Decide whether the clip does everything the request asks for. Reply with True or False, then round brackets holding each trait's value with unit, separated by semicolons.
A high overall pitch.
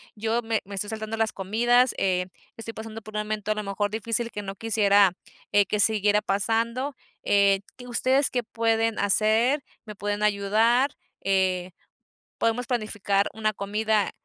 True (215 Hz)